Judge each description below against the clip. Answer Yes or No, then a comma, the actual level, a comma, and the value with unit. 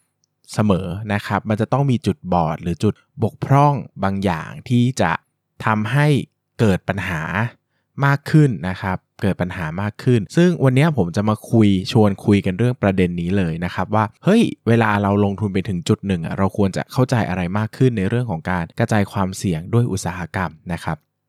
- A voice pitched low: Yes, low, 100 Hz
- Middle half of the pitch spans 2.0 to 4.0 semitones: No, average, 4.6 semitones